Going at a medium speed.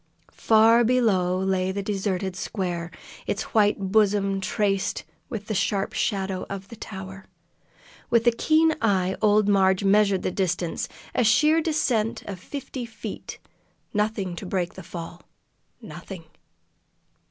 No: slow, 130 wpm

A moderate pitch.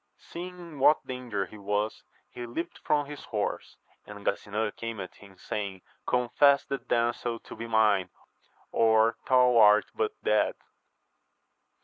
No: low, 115 Hz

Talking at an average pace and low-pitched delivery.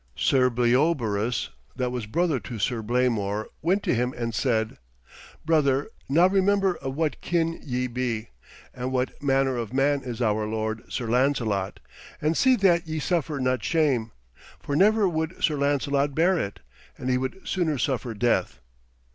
Yes: average, 160 wpm; low, 130 Hz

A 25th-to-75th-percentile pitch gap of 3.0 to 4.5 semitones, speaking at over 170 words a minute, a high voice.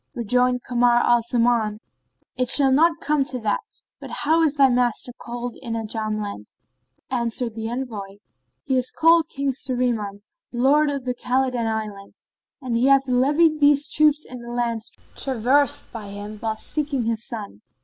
No: average, 3.3 semitones; average, 160 wpm; high, 245 Hz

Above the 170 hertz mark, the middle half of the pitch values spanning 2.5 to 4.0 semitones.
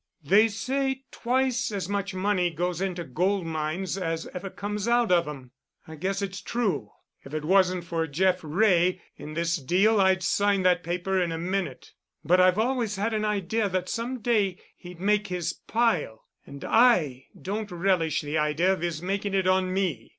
Yes: medium, 185 Hz; average, 3.3 semitones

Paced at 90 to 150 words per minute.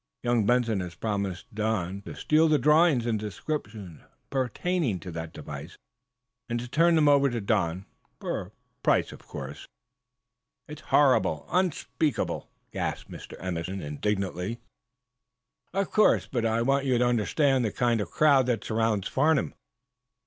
Yes: average, 145 wpm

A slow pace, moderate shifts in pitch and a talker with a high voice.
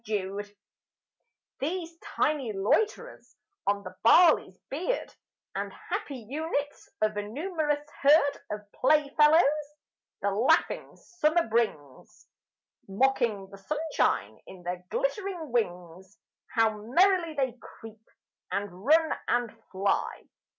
No: slow, 105 wpm; wide, 7.3 semitones; very high, 260 Hz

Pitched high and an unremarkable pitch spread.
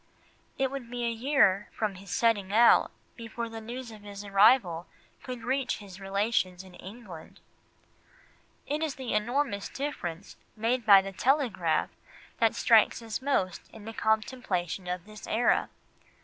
Yes: high, 220 Hz; average, 4.0 semitones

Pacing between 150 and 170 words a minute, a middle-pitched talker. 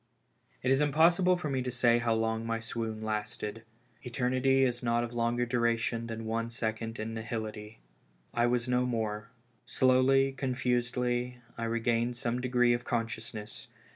No: average, 155 wpm; low, 120 Hz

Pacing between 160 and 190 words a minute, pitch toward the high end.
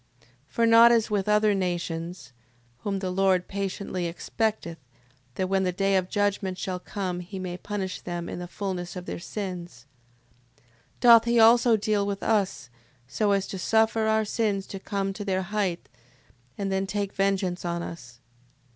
Yes: average, 175 wpm; high, 195 Hz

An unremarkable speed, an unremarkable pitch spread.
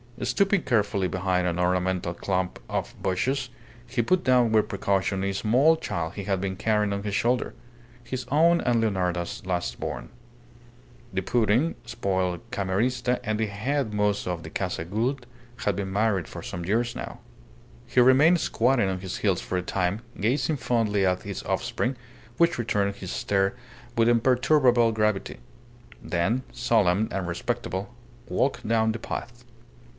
Yes: average, 155 wpm; average, 4.6 semitones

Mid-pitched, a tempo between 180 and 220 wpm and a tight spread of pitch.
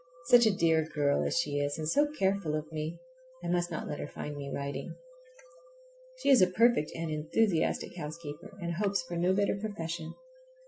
No: medium, 170 Hz; average, 185 wpm; average, 4.0 semitones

